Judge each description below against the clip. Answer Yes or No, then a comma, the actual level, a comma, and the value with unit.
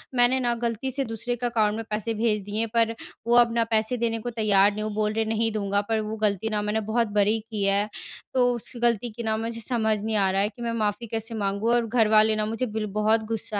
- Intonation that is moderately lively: No, narrow, 1.7 semitones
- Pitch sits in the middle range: No, high, 220 Hz